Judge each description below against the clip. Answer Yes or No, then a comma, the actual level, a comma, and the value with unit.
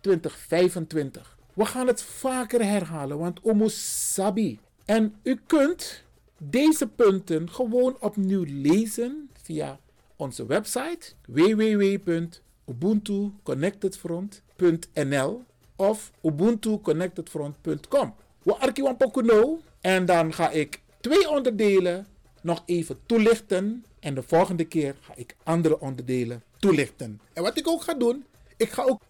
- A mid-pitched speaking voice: No, high, 195 Hz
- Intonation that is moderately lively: No, wide, 6.5 semitones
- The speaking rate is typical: No, slow, 105 wpm